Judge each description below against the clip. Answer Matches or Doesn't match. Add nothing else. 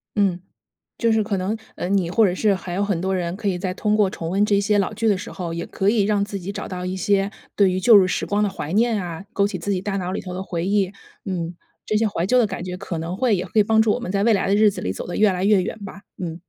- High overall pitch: Matches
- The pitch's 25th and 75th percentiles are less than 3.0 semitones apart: Matches